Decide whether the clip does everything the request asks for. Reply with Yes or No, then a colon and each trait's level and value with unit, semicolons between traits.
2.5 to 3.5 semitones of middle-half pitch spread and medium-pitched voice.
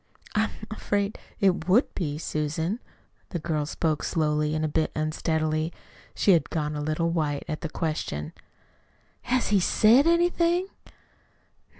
No: average, 4.9 semitones; medium, 160 Hz